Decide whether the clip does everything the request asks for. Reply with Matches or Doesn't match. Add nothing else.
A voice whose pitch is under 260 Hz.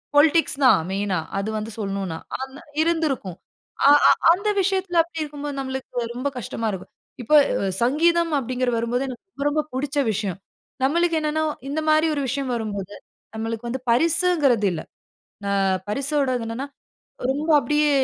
Doesn't match